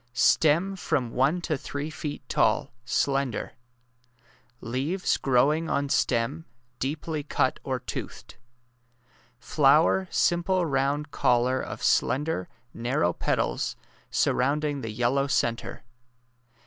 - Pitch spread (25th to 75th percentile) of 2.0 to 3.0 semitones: No, average, 3.5 semitones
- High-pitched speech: No, medium, 140 Hz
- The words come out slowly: Yes, slow, 105 wpm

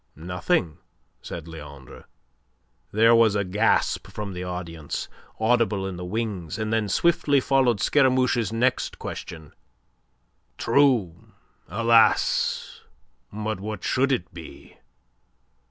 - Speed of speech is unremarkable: No, slow, 105 wpm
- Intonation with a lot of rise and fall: No, average, 4.7 semitones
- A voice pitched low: Yes, low, 105 Hz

